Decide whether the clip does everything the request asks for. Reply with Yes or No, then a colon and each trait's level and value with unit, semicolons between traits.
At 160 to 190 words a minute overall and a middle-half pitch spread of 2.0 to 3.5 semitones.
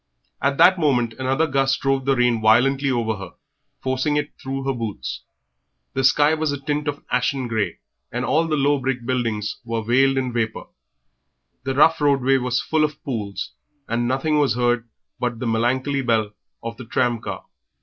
Yes: average, 180 wpm; average, 2.9 semitones